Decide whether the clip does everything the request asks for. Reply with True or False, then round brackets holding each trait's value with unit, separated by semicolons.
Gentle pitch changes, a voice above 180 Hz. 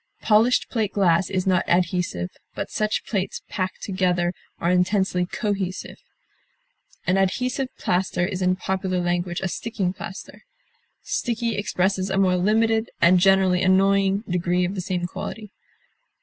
True (2.0 semitones; 190 Hz)